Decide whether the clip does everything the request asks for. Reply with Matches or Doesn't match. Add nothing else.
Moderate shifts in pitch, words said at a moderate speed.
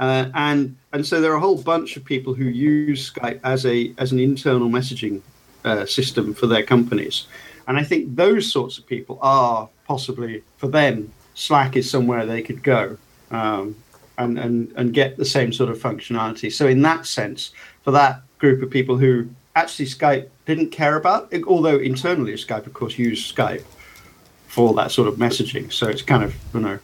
Matches